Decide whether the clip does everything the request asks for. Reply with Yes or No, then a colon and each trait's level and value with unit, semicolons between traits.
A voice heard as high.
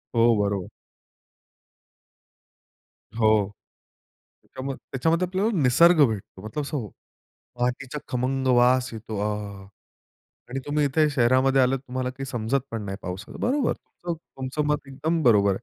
No: low, 130 Hz